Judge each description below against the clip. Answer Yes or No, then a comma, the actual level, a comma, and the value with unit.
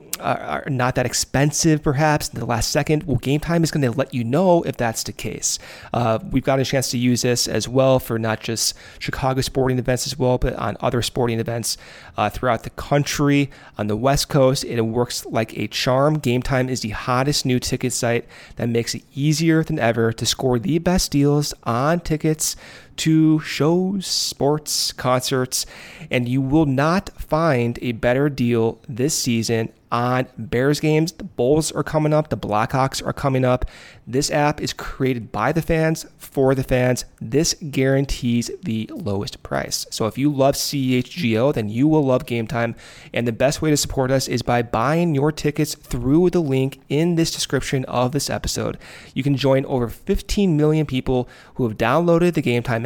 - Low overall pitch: Yes, low, 130 Hz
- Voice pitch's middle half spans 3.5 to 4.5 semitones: Yes, average, 3.9 semitones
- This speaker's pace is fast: No, average, 190 wpm